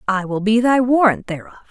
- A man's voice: No, female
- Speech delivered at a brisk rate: Yes, fast, 210 wpm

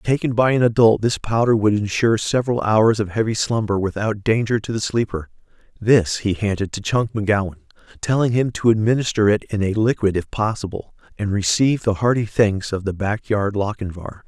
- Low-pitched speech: Yes, low, 105 Hz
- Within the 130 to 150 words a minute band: No, average, 180 wpm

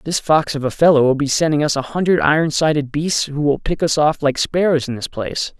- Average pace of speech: No, fast, 255 wpm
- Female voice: No, male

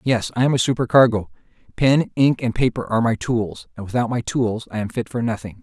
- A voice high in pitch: No, low, 120 Hz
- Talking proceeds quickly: Yes, fast, 225 wpm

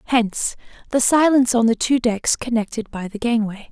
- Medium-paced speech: Yes, average, 180 wpm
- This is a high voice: Yes, high, 235 Hz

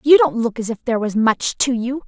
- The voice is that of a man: No, female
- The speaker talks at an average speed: No, fast, 290 wpm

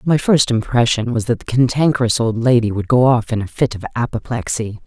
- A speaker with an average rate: No, fast, 210 wpm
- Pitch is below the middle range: Yes, low, 120 Hz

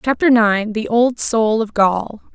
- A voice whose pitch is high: Yes, high, 225 Hz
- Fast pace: No, average, 155 wpm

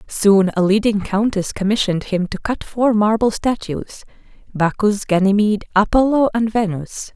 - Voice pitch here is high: Yes, high, 205 Hz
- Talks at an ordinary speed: No, slow, 125 wpm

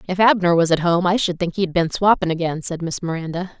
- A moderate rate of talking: No, fast, 250 wpm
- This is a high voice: No, medium, 175 Hz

